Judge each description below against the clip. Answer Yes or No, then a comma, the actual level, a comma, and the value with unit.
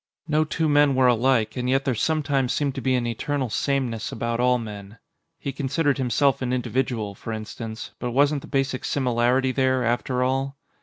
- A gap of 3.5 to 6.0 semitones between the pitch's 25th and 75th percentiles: No, narrow, 2.5 semitones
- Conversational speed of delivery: Yes, average, 185 wpm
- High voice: No, low, 130 Hz